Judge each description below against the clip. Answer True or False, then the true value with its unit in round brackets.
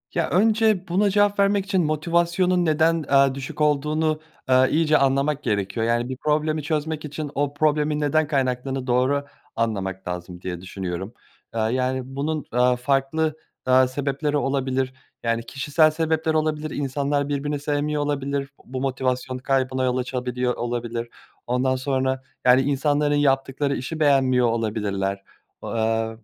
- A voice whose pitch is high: False (135 Hz)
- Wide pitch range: False (3.3 semitones)